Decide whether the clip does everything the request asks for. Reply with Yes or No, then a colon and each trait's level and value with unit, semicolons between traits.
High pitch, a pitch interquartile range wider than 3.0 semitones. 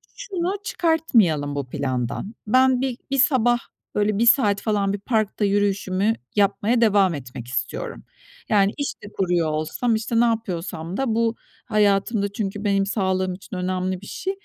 Yes: high, 205 Hz; average, 3.8 semitones